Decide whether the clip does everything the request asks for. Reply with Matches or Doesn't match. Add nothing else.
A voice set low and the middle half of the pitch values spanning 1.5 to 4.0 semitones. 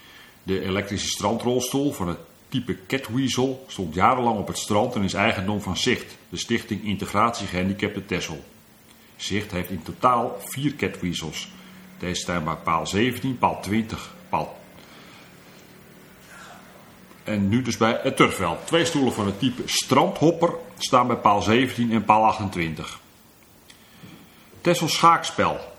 Doesn't match